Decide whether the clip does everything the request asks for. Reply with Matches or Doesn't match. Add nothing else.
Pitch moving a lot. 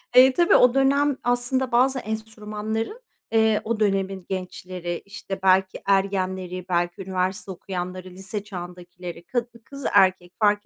Doesn't match